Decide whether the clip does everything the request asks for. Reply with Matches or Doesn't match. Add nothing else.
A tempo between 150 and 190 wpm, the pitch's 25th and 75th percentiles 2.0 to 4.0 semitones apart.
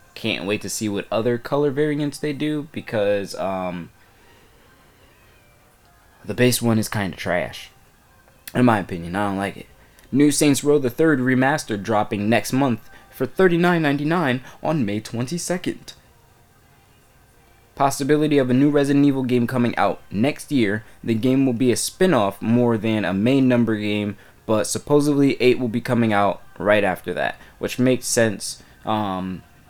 Doesn't match